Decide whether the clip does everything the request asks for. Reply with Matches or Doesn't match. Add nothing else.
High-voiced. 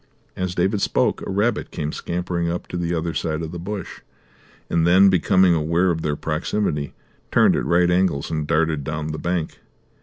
Doesn't match